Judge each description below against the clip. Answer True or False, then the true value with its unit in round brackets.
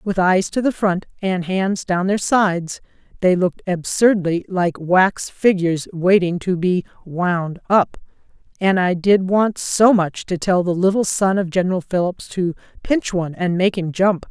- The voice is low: False (185 Hz)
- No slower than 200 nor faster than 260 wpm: False (175 wpm)